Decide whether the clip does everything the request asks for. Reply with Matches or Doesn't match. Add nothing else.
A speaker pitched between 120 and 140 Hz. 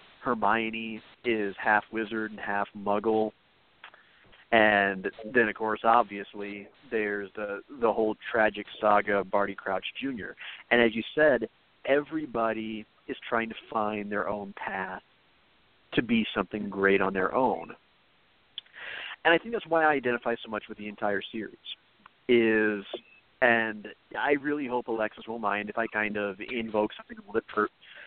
Doesn't match